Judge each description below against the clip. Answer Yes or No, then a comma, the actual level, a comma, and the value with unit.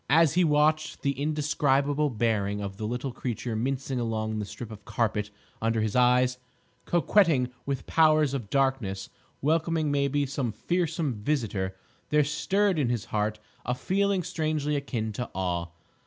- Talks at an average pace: Yes, average, 155 wpm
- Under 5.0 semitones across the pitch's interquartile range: No, wide, 5.6 semitones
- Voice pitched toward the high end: No, low, 135 Hz